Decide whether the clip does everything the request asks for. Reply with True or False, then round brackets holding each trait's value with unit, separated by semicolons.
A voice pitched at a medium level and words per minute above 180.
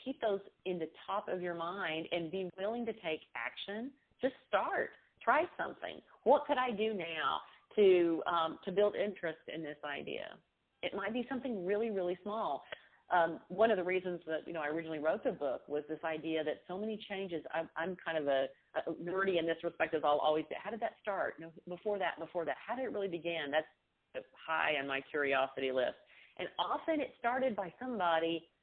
True (180 Hz; 205 wpm)